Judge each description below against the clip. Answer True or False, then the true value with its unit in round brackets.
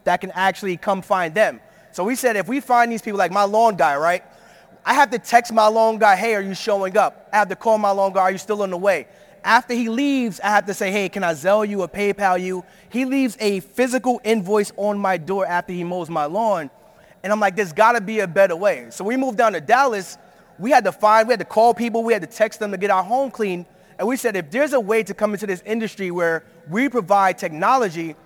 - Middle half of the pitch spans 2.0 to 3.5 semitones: True (3.1 semitones)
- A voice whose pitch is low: False (205 Hz)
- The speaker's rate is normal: False (260 wpm)